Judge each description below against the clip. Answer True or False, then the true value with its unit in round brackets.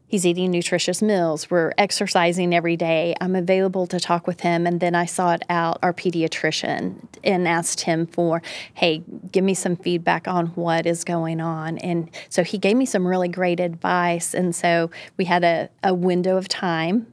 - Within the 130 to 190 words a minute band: True (185 wpm)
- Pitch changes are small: True (1.5 semitones)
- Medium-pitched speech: True (175 Hz)